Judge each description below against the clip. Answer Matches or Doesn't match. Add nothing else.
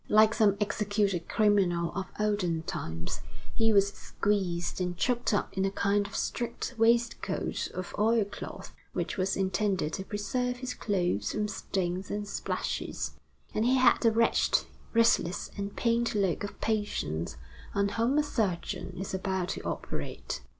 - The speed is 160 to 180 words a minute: Doesn't match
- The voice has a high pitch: Matches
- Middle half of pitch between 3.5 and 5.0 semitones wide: Doesn't match